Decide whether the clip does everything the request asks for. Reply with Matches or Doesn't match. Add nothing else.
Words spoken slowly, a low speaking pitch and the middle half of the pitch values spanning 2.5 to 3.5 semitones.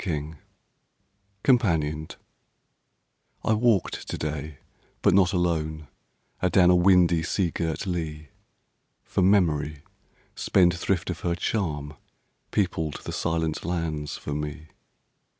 Matches